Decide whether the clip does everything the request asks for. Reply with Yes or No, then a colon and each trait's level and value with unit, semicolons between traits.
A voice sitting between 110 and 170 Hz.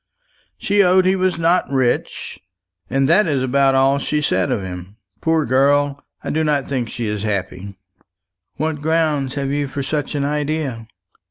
Yes: medium, 140 Hz